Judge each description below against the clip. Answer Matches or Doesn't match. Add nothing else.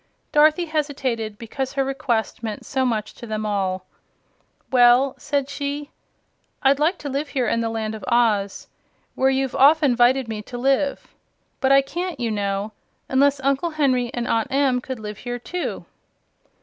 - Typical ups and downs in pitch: Matches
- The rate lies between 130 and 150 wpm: Doesn't match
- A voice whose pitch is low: Doesn't match